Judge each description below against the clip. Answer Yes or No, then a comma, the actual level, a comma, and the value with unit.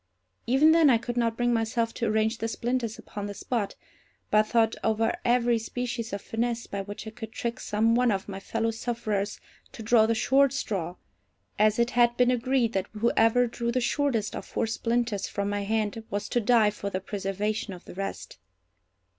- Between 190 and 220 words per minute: Yes, average, 195 wpm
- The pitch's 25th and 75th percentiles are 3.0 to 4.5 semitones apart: No, narrow, 2.4 semitones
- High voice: Yes, high, 225 Hz